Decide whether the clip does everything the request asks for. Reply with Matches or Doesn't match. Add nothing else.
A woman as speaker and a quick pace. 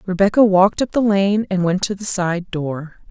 Matches